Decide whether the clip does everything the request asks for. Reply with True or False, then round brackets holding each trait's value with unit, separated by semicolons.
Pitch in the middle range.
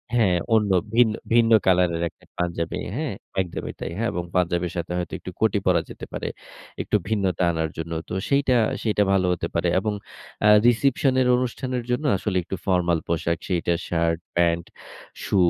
False (95 Hz)